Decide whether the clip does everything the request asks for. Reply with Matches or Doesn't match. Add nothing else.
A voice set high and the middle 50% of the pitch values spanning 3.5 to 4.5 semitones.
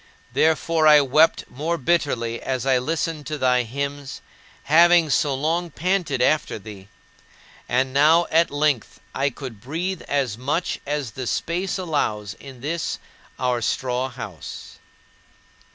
Doesn't match